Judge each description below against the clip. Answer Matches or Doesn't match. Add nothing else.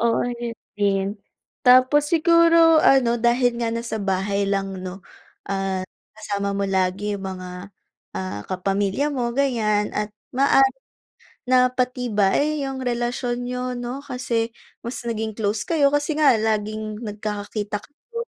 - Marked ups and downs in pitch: Doesn't match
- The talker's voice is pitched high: Matches